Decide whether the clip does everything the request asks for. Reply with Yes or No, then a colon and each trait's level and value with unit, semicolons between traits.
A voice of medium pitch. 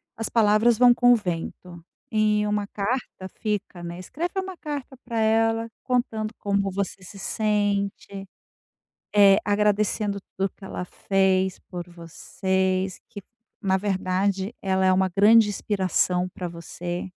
No: high, 200 Hz